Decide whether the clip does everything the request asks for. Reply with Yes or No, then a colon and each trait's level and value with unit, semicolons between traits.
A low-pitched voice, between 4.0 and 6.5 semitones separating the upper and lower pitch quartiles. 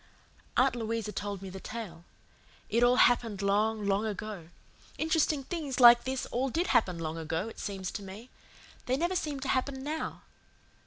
No: high, 225 Hz; average, 4.9 semitones